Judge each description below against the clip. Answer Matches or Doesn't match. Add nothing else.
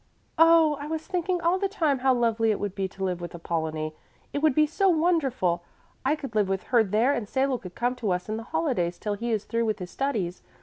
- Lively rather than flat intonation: Matches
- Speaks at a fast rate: Matches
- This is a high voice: Matches